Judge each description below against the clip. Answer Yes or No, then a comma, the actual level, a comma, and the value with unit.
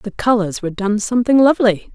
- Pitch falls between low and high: No, high, 220 Hz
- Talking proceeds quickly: No, average, 185 wpm